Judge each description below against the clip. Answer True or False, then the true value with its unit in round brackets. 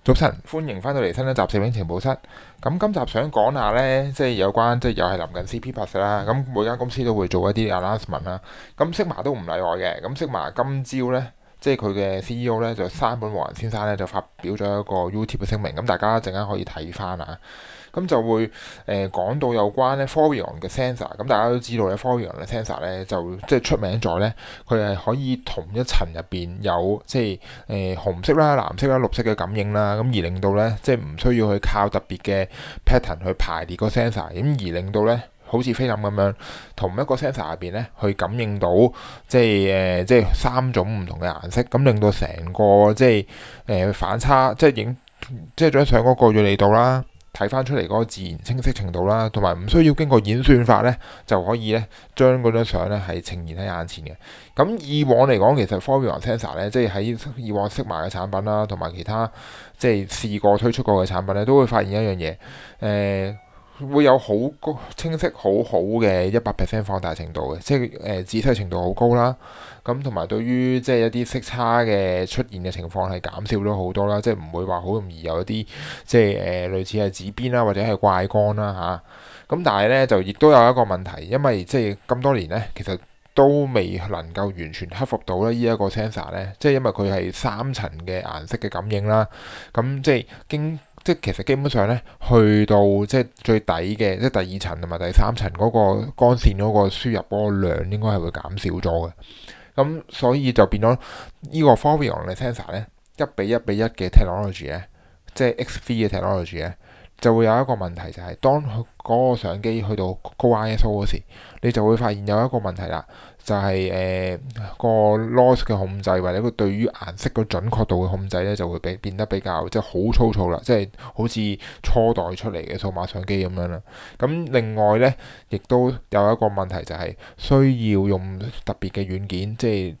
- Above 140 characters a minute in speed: True (345 characters per minute)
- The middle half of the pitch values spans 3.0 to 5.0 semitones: True (4.4 semitones)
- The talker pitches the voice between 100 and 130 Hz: True (105 Hz)